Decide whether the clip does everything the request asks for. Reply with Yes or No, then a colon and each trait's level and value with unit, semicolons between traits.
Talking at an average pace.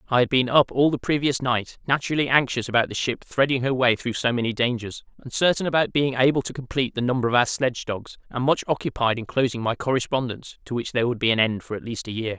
No: fast, 245 wpm